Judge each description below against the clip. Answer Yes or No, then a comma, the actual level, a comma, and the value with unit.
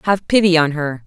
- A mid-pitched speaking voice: Yes, medium, 165 Hz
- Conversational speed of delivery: No, fast, 225 wpm